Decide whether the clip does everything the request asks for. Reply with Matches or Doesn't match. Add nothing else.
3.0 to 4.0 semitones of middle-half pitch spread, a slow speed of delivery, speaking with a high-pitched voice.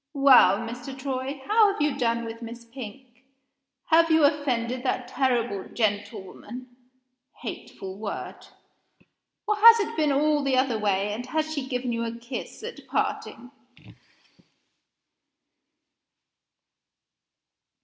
Matches